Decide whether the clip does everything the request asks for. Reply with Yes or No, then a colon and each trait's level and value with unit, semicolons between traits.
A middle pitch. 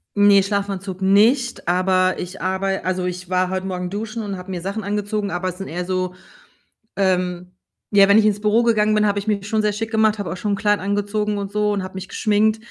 No: high, 200 Hz